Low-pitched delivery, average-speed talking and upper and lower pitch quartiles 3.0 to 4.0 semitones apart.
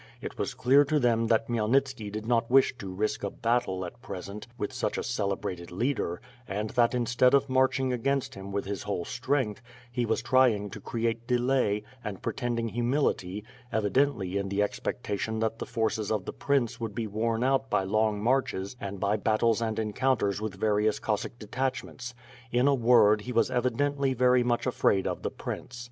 Yes: low, 115 Hz; average, 190 wpm; average, 3.4 semitones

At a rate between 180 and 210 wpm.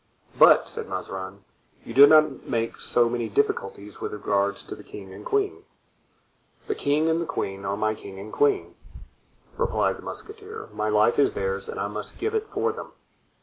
Yes: average, 185 wpm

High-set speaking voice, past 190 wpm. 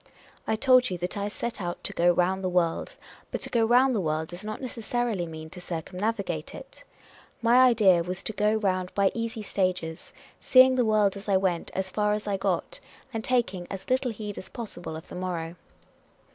Yes: high, 200 Hz; average, 200 wpm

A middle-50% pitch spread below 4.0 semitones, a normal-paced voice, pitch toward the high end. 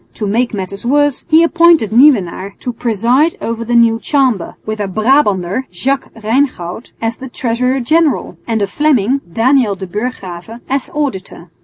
No: average, 5.0 semitones; average, 150 wpm; high, 235 Hz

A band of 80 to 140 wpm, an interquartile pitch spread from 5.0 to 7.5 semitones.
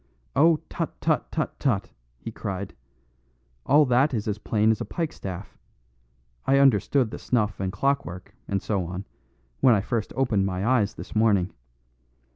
No: average, 155 wpm; wide, 5.5 semitones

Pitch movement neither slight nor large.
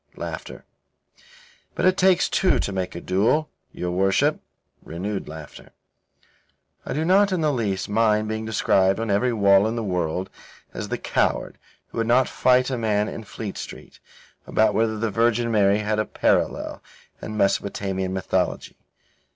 Yes: average, 3.3 semitones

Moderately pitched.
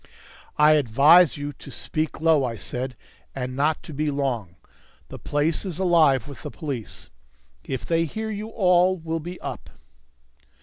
Yes: medium, 150 Hz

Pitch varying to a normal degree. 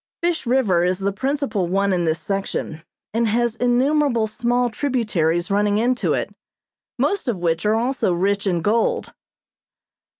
Yes: average, 4.7 semitones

